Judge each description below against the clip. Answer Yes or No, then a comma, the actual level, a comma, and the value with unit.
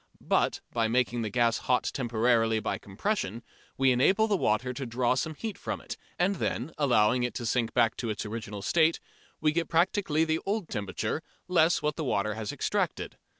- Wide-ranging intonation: Yes, wide, 6.0 semitones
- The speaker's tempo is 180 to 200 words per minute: Yes, average, 190 wpm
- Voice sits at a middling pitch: No, low, 125 Hz